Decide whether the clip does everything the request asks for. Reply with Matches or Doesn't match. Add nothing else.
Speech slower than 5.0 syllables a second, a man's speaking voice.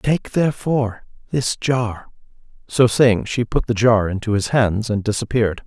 Matches